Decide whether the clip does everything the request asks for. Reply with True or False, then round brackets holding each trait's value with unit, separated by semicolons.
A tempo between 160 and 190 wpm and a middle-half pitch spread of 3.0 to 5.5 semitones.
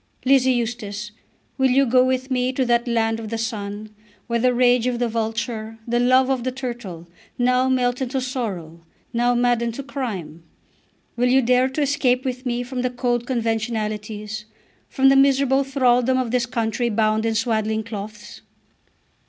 False (170 wpm; 2.4 semitones)